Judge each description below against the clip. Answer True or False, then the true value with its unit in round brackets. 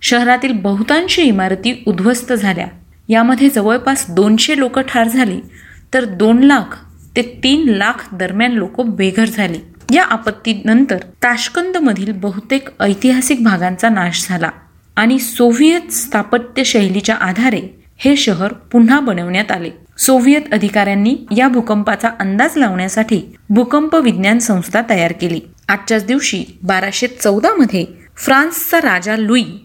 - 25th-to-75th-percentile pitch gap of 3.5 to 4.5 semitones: True (4.2 semitones)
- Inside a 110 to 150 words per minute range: True (115 wpm)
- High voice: True (230 Hz)